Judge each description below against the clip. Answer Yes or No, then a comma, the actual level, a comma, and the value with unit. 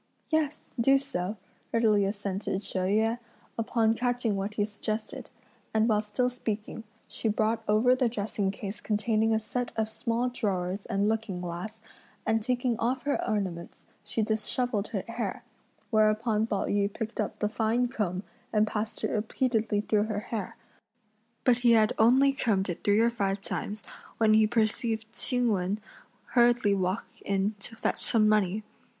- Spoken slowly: No, average, 160 wpm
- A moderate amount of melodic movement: No, narrow, 2.2 semitones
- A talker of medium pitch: No, high, 220 Hz